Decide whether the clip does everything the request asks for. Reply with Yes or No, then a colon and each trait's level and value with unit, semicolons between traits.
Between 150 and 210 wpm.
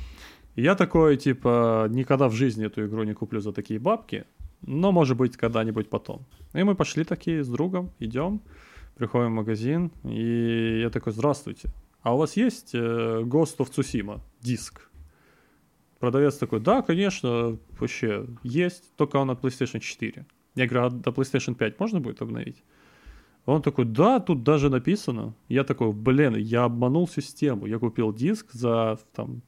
Yes: average, 155 wpm